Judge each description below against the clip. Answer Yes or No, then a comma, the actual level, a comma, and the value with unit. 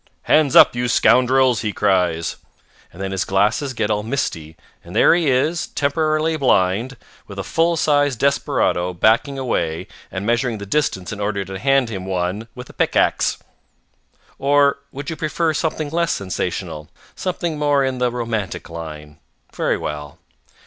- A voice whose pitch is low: Yes, low, 120 Hz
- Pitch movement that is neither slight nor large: No, wide, 6.9 semitones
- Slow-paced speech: No, average, 155 wpm